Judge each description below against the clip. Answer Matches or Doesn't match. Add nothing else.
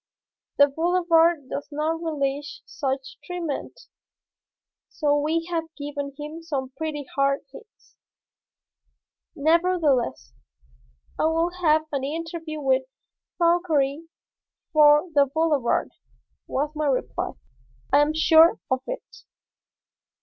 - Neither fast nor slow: Doesn't match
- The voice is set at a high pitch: Matches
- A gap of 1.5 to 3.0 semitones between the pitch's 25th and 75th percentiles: Matches